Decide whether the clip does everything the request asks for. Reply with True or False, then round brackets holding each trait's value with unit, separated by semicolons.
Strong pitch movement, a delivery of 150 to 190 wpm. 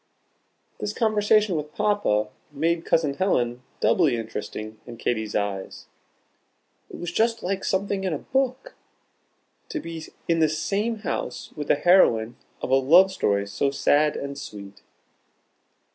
False (8.6 semitones; 140 wpm)